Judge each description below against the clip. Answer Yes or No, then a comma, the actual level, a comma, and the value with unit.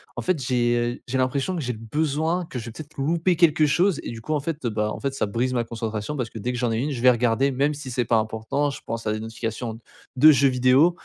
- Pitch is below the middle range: Yes, low, 125 Hz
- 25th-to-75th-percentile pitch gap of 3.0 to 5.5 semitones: Yes, average, 4.4 semitones